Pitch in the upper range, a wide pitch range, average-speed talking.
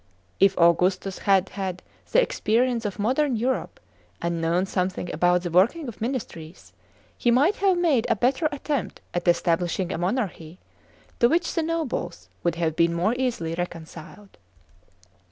Yes: high, 195 Hz; wide, 6.8 semitones; average, 150 wpm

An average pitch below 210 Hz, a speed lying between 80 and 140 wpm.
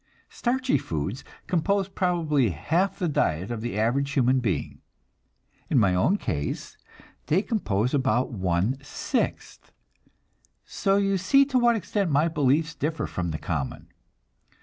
Yes: medium, 140 Hz; slow, 135 wpm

